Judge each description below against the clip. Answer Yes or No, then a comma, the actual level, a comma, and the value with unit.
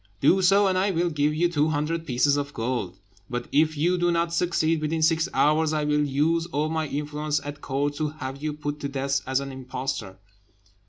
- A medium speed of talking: No, fast, 210 wpm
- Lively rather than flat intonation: No, average, 2.7 semitones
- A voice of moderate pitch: Yes, medium, 150 Hz